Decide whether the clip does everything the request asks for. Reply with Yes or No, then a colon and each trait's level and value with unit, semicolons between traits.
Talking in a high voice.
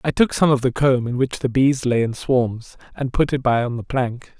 No: low, 130 Hz